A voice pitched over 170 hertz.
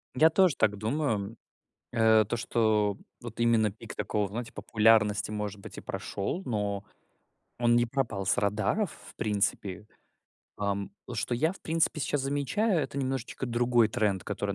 No: low, 115 Hz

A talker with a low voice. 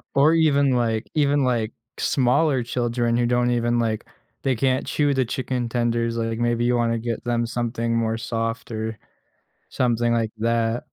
Yes: low, 120 Hz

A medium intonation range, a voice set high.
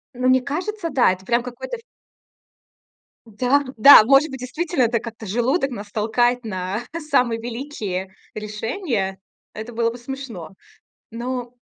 Yes: average, 3.6 semitones; high, 240 Hz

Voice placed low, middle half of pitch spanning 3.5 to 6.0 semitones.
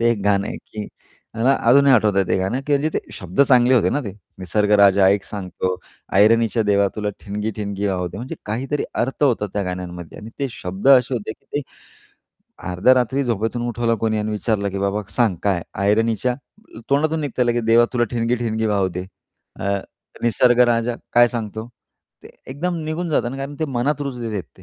Yes: low, 115 Hz; average, 3.8 semitones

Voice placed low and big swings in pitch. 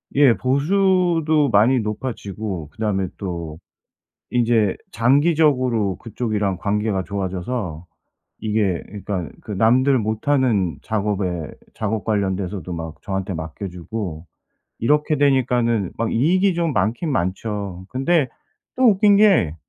Yes: low, 110 Hz; wide, 6.0 semitones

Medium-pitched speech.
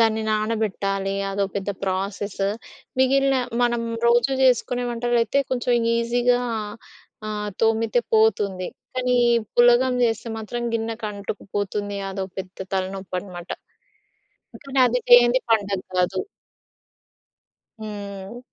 No: high, 220 Hz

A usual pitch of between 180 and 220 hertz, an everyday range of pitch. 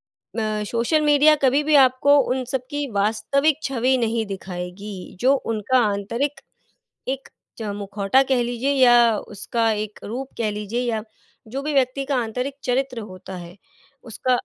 No: high, 240 Hz; average, 4.1 semitones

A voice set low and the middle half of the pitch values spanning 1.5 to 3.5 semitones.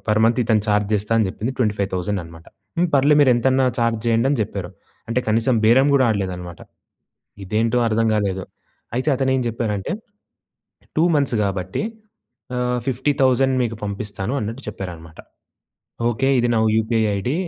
No: low, 115 Hz; average, 4.0 semitones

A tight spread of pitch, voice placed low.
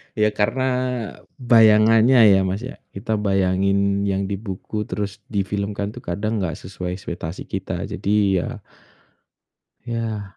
Yes: narrow, 2.2 semitones; low, 100 Hz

